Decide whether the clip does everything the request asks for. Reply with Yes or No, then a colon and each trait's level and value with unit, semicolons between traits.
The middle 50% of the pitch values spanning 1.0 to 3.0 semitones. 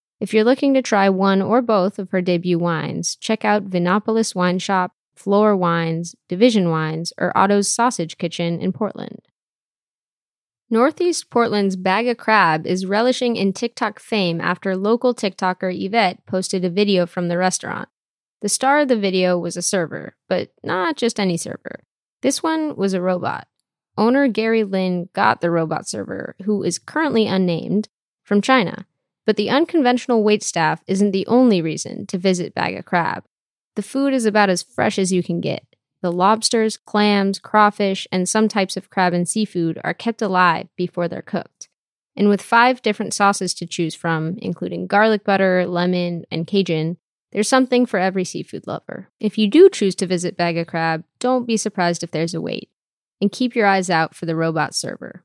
No: average, 3.7 semitones